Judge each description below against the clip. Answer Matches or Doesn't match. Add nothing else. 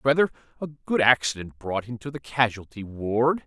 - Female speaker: Doesn't match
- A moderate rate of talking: Matches